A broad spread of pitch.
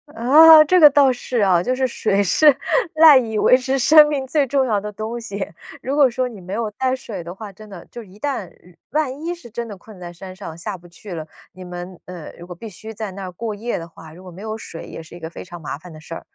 Yes: wide, 6.1 semitones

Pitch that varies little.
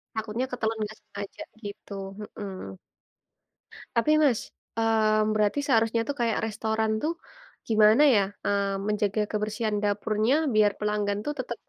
Yes: narrow, 1.5 semitones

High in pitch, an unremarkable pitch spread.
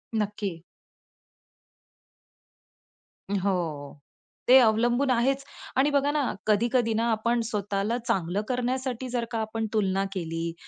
Yes: high, 225 Hz; average, 3.9 semitones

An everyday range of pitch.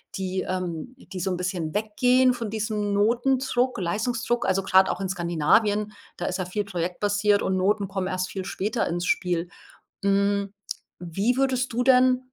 Yes: average, 4.2 semitones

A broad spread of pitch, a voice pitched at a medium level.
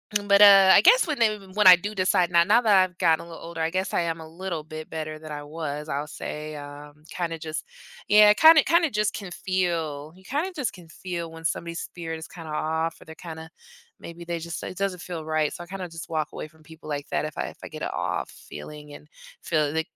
No: average, 3.3 semitones; medium, 165 Hz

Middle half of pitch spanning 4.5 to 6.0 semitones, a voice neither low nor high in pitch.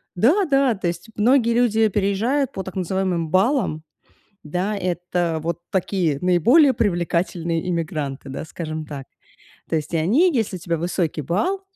Yes: average, 5.2 semitones; medium, 180 Hz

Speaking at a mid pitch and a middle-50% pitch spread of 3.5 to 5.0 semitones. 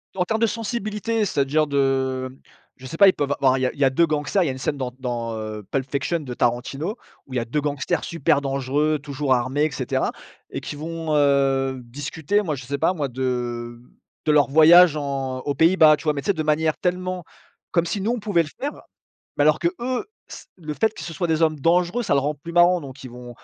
Yes: medium, 145 Hz; average, 4.2 semitones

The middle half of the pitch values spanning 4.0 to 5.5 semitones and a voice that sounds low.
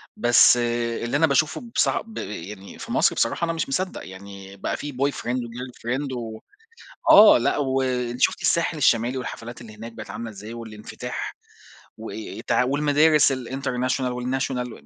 No: average, 3.1 semitones; low, 125 Hz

